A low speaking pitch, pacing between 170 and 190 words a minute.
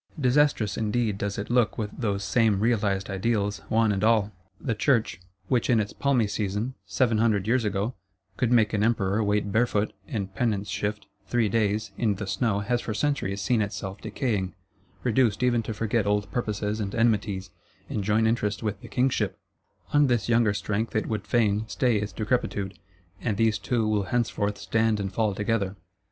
Yes: low, 110 Hz; average, 175 wpm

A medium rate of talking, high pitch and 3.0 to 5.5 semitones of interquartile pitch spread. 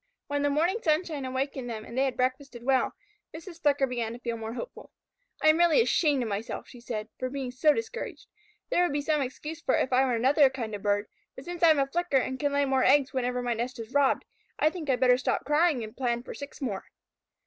No: fast, 245 wpm; very high, 265 Hz; average, 3.5 semitones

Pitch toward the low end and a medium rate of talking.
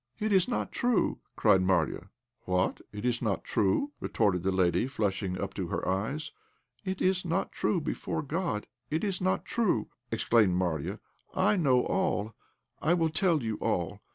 Yes: low, 125 Hz; average, 155 wpm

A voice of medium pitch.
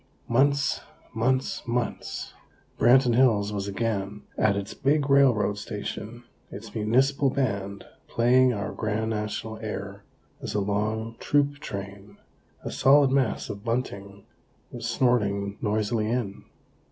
No: low, 110 Hz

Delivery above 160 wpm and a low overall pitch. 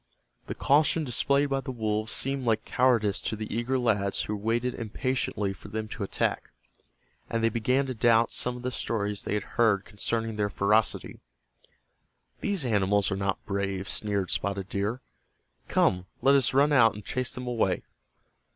Yes: average, 170 wpm; low, 110 Hz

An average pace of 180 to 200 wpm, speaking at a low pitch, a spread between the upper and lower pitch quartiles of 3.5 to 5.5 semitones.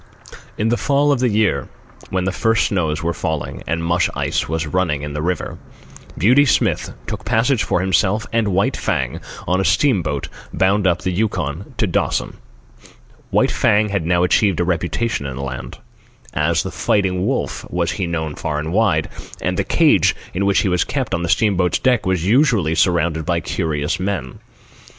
Yes: average, 185 wpm; very low, 90 Hz; average, 4.5 semitones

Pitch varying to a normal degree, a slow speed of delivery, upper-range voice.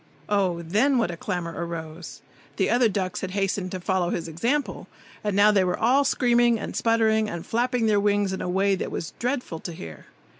No: average, 4.4 semitones; average, 200 wpm; high, 200 Hz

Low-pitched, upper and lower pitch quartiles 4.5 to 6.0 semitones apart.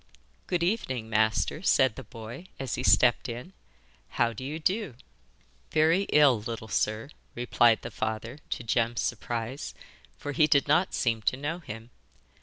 Yes: low, 125 Hz; average, 5.0 semitones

